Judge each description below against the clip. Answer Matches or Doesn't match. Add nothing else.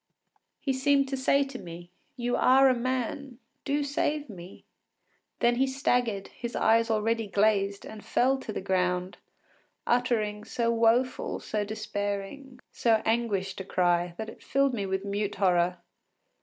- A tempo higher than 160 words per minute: Doesn't match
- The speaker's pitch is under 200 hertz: Doesn't match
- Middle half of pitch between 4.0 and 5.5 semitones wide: Matches